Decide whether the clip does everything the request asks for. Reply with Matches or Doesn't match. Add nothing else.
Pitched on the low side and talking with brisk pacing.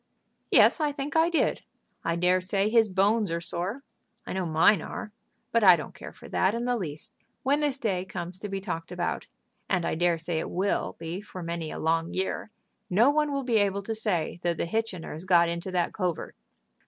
Doesn't match